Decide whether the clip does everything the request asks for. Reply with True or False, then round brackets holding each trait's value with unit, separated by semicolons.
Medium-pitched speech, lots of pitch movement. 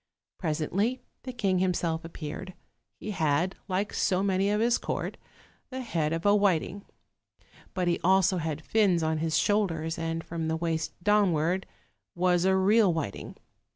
False (180 Hz; 3.6 semitones)